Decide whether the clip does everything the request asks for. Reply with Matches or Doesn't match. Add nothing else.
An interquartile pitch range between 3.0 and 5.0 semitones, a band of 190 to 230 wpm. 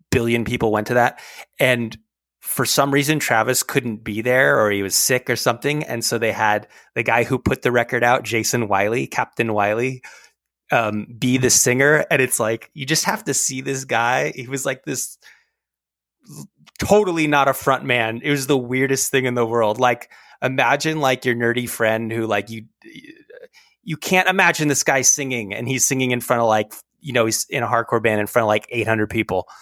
Matches